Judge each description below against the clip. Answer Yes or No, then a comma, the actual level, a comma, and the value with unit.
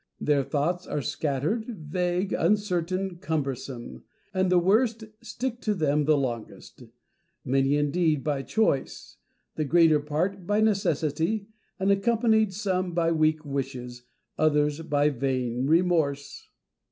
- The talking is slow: Yes, slow, 120 wpm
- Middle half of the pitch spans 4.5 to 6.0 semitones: Yes, average, 5.1 semitones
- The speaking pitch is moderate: Yes, medium, 160 Hz